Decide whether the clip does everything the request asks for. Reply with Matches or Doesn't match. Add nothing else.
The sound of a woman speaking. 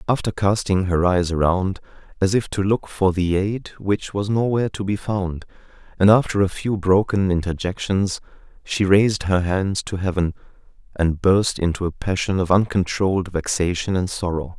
Doesn't match